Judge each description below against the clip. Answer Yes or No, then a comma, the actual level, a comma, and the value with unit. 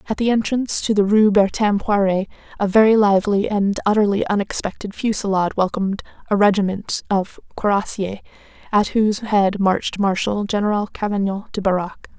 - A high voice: Yes, high, 205 Hz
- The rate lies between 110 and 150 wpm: Yes, average, 145 wpm